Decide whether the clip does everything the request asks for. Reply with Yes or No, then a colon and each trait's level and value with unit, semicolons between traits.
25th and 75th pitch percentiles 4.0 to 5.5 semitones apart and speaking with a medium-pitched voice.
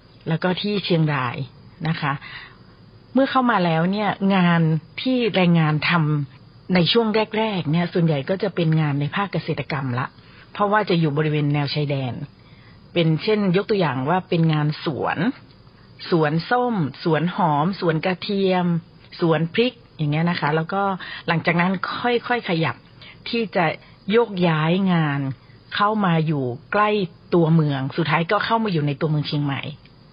Yes: average, 4.5 semitones; medium, 170 Hz